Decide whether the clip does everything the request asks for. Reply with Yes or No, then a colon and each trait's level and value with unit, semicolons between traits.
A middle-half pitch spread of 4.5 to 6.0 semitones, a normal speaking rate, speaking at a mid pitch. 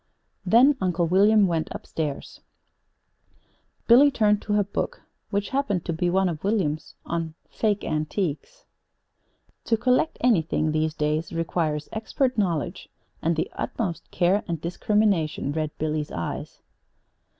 No: average, 5.1 semitones; slow, 130 wpm; medium, 175 Hz